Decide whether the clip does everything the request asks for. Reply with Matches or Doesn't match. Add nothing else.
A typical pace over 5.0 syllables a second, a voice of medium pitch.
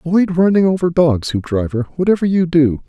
Matches